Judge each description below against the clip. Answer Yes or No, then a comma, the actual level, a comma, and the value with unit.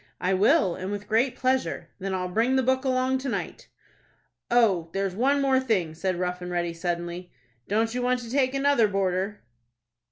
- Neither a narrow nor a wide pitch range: No, wide, 5.9 semitones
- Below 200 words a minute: Yes, average, 185 wpm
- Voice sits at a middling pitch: No, high, 205 Hz